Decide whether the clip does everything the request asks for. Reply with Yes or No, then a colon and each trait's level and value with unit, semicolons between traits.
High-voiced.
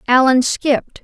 Yes: very high, 260 Hz